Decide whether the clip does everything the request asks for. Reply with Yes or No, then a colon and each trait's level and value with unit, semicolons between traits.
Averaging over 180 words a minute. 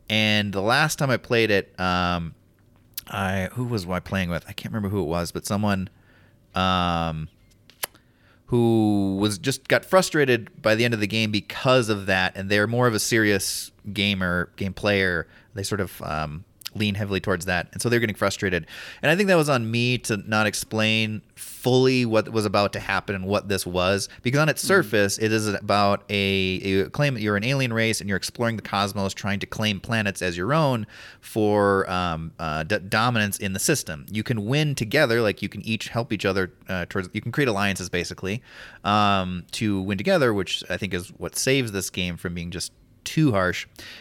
Yes: fast, 205 wpm